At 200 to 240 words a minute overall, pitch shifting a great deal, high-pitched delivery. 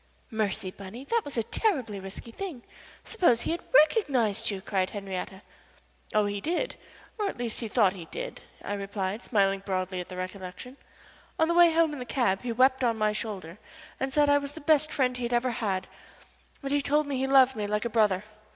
Yes: fast, 205 wpm; wide, 6.1 semitones; high, 235 Hz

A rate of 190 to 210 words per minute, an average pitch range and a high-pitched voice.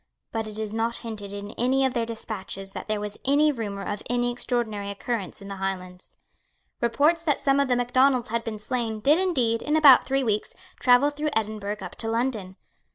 Yes: average, 200 wpm; average, 3.9 semitones; high, 230 Hz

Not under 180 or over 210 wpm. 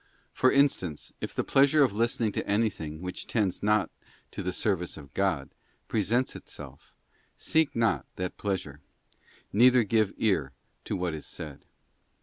No: average, 150 wpm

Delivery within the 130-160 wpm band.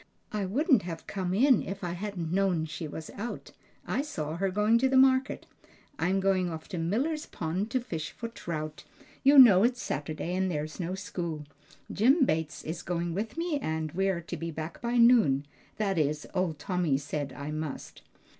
No: average, 185 wpm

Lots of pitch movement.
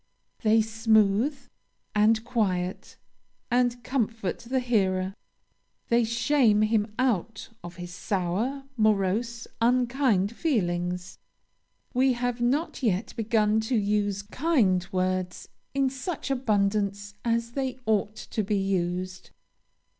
No: average, 3.9 semitones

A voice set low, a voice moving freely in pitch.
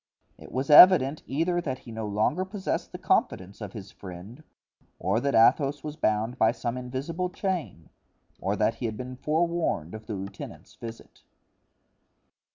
Yes: low, 125 Hz; wide, 6.1 semitones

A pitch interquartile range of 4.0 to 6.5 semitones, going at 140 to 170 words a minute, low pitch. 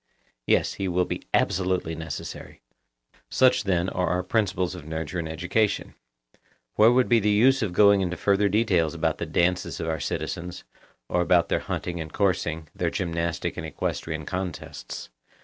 No: average, 3.2 semitones; average, 165 wpm; very low, 90 Hz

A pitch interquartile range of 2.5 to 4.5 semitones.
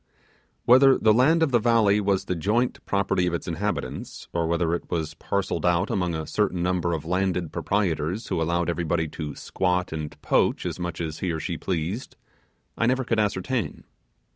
Yes: average, 3.8 semitones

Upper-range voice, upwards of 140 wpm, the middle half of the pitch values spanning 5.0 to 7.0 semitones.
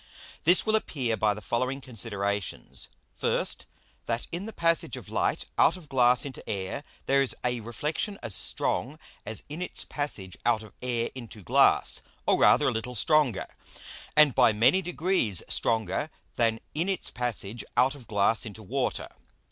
No: low, 120 Hz; average, 165 wpm; average, 5.3 semitones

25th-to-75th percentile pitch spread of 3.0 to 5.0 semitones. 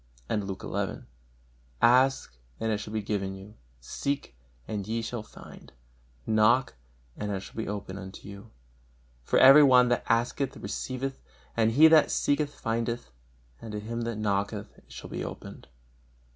Yes: average, 3.5 semitones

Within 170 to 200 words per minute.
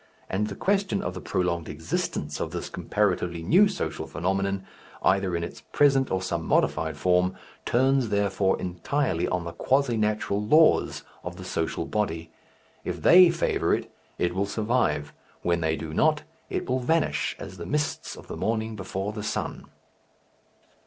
No: average, 160 wpm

